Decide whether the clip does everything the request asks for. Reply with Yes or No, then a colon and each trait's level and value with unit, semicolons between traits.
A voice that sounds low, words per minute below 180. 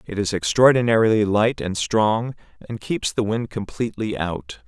Yes: low, 105 Hz; average, 155 wpm